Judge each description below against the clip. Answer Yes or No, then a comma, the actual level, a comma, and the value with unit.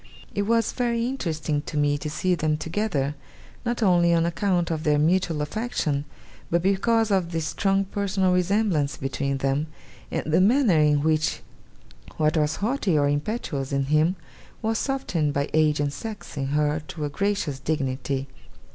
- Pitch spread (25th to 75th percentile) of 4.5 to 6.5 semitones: Yes, average, 5.1 semitones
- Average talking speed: Yes, average, 165 wpm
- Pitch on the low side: No, medium, 160 Hz